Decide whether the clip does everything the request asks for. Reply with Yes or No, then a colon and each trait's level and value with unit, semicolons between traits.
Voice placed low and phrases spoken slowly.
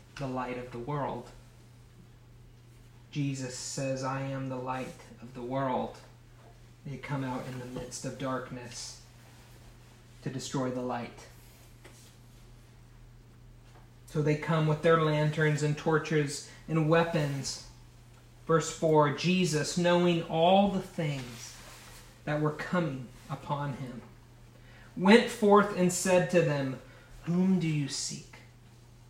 Yes: low, 125 Hz; slow, 120 wpm